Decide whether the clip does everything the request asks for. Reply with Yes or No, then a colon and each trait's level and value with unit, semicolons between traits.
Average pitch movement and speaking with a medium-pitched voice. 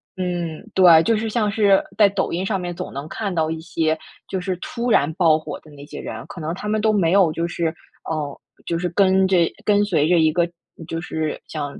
Yes: average, 3.7 semitones; medium, 175 Hz